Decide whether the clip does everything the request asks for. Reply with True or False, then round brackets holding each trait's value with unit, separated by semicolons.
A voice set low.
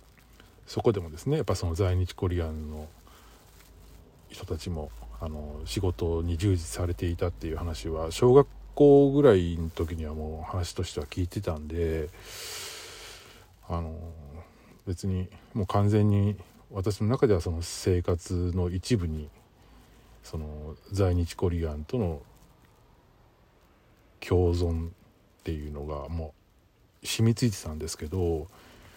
True (90 Hz)